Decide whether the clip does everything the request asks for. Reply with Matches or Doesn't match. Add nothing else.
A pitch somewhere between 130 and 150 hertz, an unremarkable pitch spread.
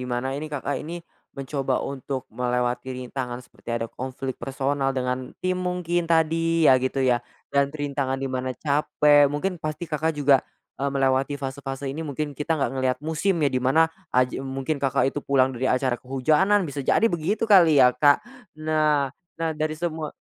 Matches